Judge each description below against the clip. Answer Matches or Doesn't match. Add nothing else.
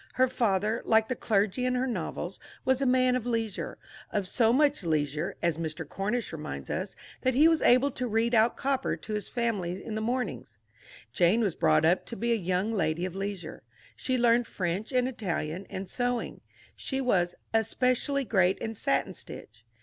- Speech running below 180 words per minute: Doesn't match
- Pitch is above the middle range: Matches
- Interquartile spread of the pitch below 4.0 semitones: Doesn't match